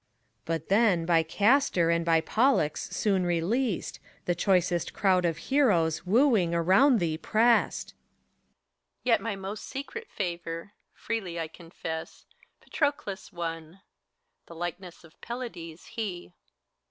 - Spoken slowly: Yes, slow, 125 wpm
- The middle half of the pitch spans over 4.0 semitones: Yes, average, 4.9 semitones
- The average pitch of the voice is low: No, medium, 180 Hz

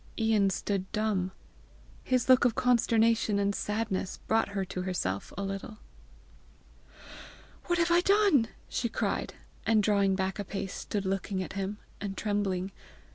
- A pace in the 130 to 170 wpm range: Yes, average, 145 wpm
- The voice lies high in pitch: Yes, high, 205 Hz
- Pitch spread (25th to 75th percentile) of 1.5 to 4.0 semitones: Yes, average, 2.7 semitones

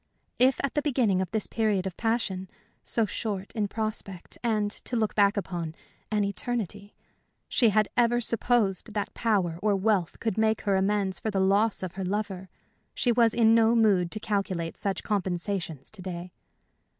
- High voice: Yes, high, 205 Hz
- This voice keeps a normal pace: Yes, average, 175 wpm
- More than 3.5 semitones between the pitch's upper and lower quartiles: No, average, 2.8 semitones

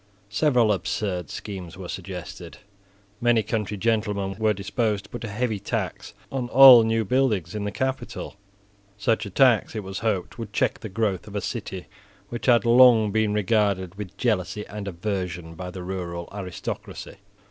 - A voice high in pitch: No, low, 105 Hz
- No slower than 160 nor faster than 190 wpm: Yes, average, 165 wpm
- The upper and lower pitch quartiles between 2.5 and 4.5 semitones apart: Yes, average, 3.2 semitones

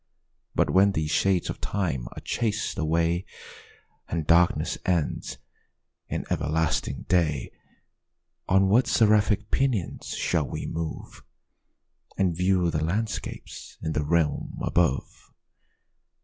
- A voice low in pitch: Yes, very low, 85 Hz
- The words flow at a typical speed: No, slow, 110 wpm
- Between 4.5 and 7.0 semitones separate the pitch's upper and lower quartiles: No, average, 3.7 semitones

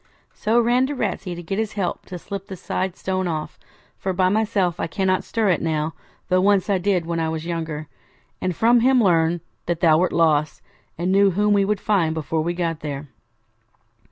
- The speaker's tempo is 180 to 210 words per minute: Yes, fast, 205 wpm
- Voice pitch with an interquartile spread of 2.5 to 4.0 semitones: Yes, average, 3.5 semitones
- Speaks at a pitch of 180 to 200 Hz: Yes, medium, 185 Hz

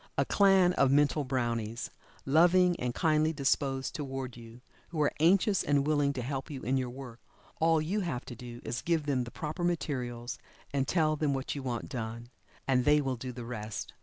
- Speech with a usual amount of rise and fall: Yes, average, 3.9 semitones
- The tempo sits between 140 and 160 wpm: No, average, 200 wpm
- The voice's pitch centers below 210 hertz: Yes, low, 135 Hz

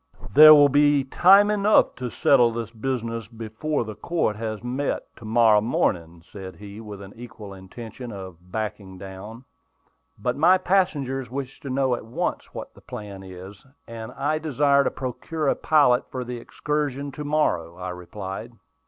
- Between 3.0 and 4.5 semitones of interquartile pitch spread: No, average, 5.3 semitones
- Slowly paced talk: No, average, 165 wpm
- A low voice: Yes, low, 120 Hz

